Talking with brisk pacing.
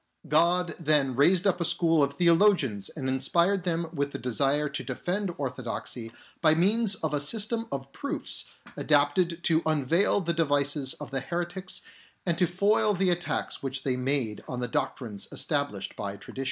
No: average, 165 wpm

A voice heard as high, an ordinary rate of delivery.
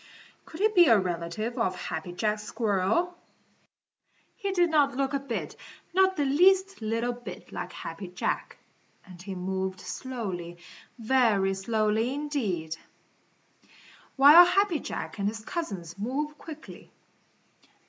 No: high, 230 Hz; slow, 125 wpm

